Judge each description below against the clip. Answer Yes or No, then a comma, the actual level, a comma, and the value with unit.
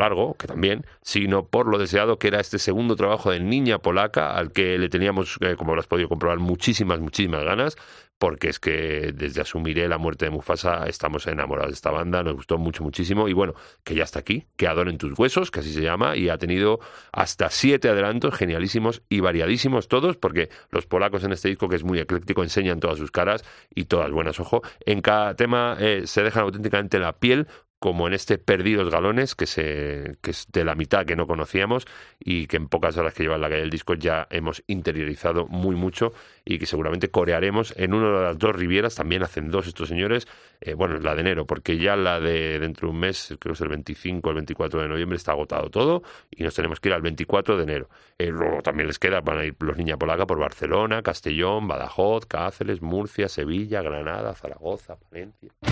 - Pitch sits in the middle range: No, very low, 90 Hz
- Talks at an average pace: No, fast, 215 wpm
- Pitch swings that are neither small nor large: Yes, average, 3.7 semitones